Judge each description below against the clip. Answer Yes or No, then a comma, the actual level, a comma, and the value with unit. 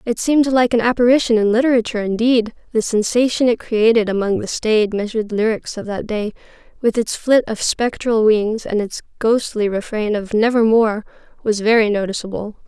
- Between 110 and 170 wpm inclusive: Yes, average, 165 wpm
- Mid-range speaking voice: No, high, 225 Hz